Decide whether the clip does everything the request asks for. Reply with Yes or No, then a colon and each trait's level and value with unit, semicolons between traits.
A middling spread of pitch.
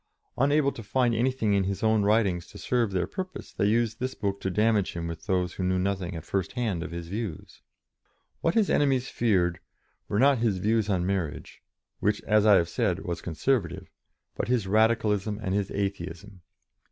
Yes: average, 4.0 semitones